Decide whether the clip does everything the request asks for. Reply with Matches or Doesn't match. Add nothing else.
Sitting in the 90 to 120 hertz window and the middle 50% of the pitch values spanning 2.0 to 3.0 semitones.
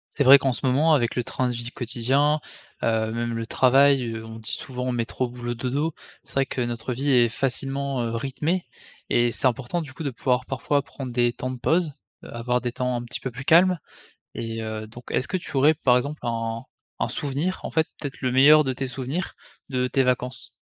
Doesn't match